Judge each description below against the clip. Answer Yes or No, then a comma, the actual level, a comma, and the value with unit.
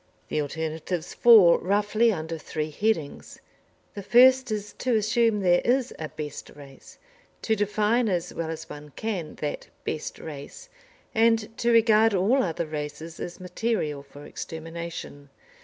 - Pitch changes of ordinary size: No, wide, 6.1 semitones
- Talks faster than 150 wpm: No, average, 140 wpm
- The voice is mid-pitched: Yes, medium, 180 Hz